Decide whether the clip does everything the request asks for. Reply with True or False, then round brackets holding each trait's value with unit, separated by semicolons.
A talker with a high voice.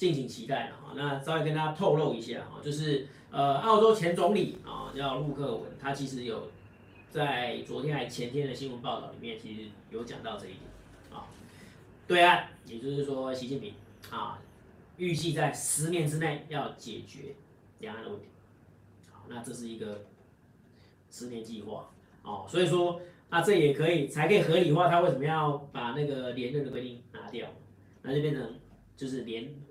False (140 Hz)